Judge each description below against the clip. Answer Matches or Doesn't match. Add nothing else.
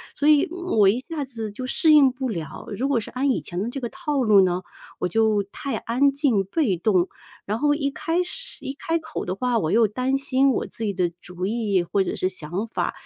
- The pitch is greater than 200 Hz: Matches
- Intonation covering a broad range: Matches